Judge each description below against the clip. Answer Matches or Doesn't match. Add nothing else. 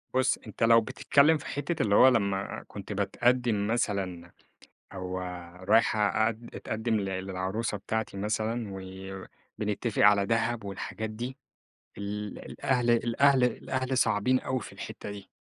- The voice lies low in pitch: Matches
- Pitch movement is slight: Doesn't match